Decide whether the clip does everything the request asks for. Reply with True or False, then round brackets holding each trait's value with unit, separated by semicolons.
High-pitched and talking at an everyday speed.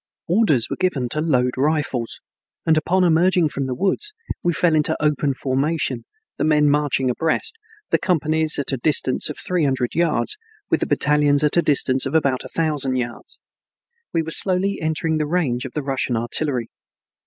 False (150 Hz; 175 wpm)